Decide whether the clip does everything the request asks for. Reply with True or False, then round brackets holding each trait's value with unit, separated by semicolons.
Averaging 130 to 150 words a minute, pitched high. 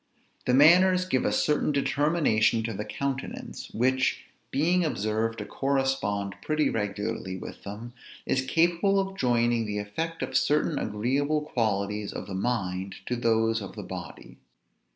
False (145 wpm; 120 Hz)